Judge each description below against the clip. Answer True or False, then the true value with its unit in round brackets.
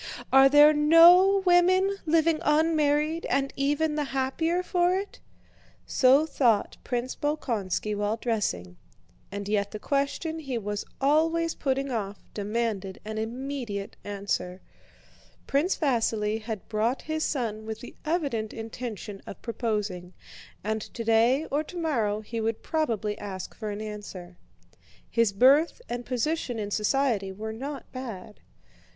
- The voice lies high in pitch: True (240 Hz)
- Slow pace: True (130 wpm)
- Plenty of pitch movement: True (6.0 semitones)